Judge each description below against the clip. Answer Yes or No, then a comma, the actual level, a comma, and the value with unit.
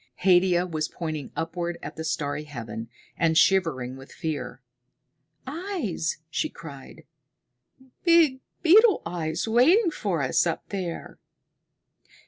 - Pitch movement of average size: No, wide, 7.7 semitones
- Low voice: No, medium, 170 Hz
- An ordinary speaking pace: No, slow, 110 wpm